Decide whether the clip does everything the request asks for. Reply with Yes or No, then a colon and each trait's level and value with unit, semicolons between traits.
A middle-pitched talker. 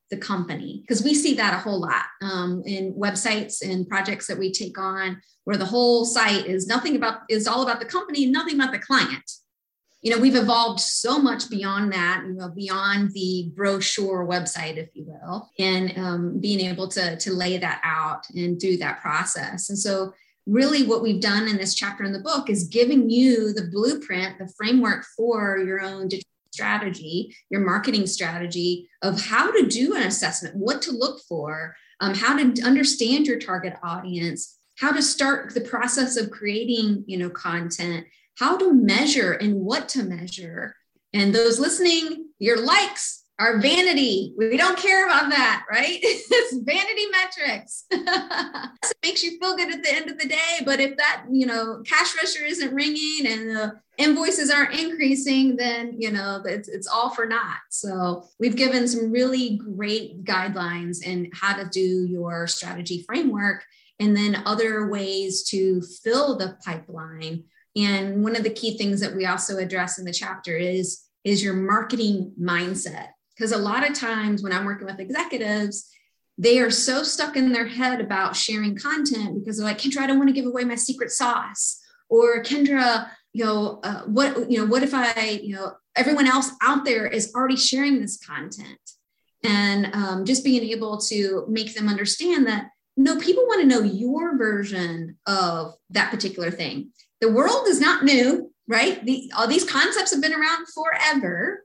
No: high, 220 Hz